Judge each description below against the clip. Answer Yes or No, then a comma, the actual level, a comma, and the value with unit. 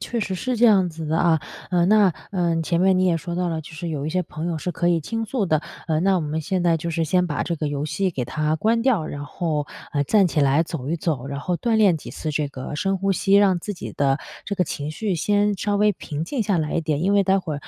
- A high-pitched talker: No, medium, 170 Hz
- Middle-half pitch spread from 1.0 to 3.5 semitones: No, average, 4.0 semitones